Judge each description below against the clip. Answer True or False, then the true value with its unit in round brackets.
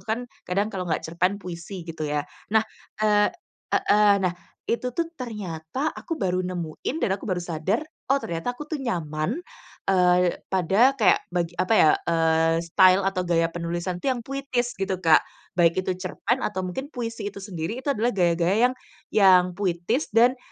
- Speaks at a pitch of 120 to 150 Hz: False (185 Hz)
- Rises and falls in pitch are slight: False (5.1 semitones)